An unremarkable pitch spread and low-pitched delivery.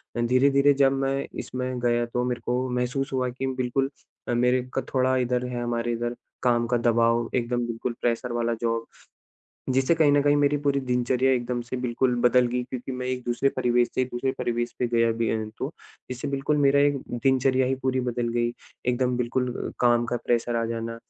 No: narrow, 1.6 semitones; low, 125 Hz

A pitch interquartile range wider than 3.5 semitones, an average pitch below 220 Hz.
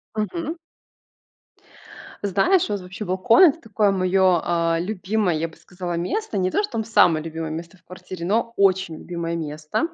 Yes: average, 4.1 semitones; medium, 185 Hz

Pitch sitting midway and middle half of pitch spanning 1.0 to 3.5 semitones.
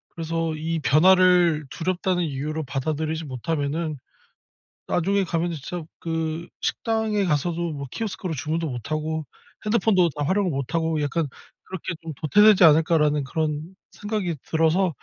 Yes: medium, 165 Hz; average, 2.7 semitones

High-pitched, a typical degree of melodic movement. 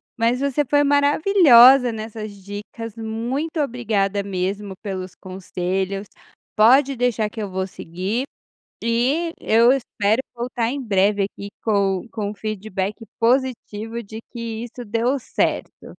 Yes: high, 225 Hz; average, 3.7 semitones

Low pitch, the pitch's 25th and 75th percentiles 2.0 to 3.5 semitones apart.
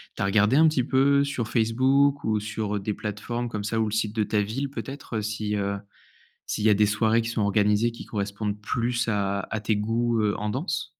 Yes: low, 110 Hz; narrow, 2.4 semitones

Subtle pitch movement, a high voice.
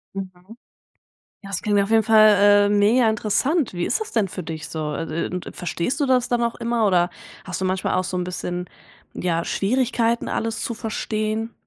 No: average, 4.0 semitones; high, 205 Hz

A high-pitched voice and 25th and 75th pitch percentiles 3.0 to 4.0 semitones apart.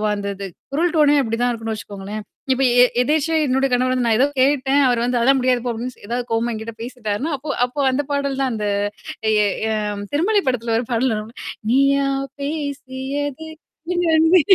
Yes: very high, 255 Hz; average, 3.6 semitones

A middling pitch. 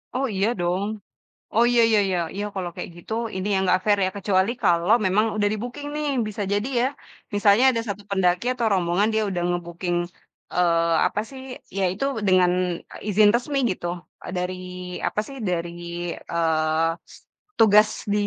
No: high, 195 Hz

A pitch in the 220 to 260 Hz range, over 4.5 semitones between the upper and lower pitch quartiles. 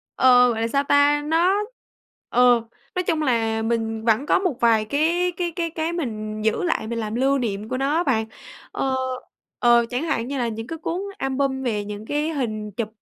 Yes: very high, 250 Hz; average, 5.1 semitones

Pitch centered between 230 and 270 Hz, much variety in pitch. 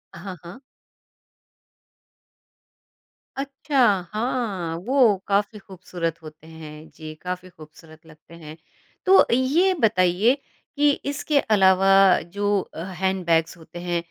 No: medium, 185 Hz; wide, 5.7 semitones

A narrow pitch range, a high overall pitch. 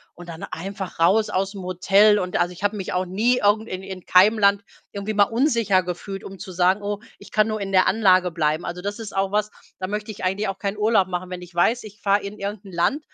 Yes: narrow, 2.3 semitones; high, 195 Hz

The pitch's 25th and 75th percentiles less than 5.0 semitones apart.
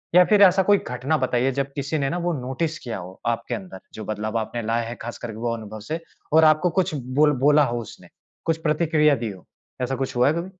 No: wide, 5.4 semitones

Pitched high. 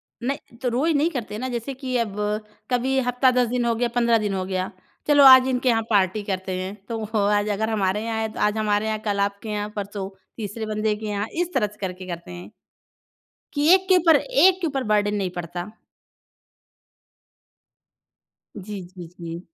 Yes: high, 215 Hz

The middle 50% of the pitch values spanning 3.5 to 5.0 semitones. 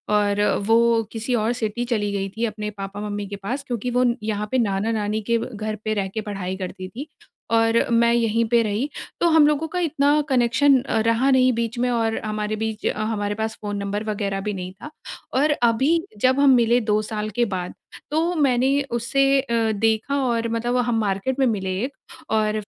No: average, 3.1 semitones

